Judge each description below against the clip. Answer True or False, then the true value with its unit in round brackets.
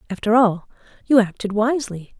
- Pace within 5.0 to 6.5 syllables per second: True (5.6 syllables/s)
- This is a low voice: False (220 Hz)